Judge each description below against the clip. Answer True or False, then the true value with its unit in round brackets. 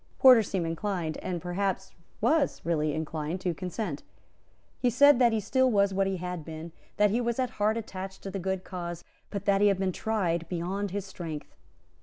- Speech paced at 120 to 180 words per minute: False (195 wpm)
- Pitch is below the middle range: False (190 Hz)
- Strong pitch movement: False (3.5 semitones)